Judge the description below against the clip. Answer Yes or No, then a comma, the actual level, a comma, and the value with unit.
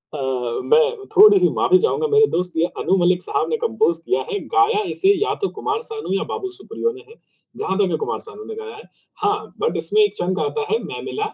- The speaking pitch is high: Yes, very high, 405 Hz